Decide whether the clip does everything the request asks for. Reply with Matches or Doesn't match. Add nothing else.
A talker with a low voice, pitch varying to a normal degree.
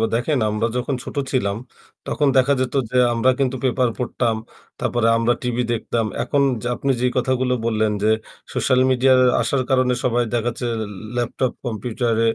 Doesn't match